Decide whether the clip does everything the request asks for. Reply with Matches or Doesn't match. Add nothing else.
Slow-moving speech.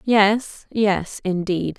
Matches